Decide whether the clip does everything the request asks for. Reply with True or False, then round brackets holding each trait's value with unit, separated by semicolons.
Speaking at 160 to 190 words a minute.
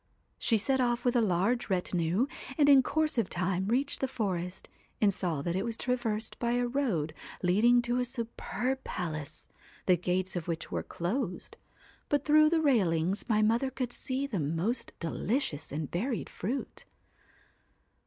True (165 wpm)